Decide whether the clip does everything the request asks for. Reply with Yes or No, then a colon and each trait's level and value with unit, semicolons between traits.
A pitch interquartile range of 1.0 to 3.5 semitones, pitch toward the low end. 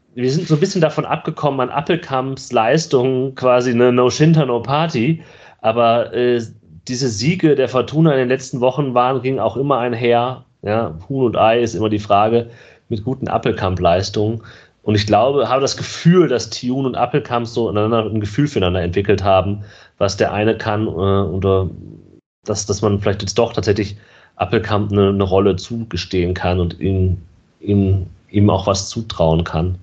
No: average, 4.5 semitones; low, 115 Hz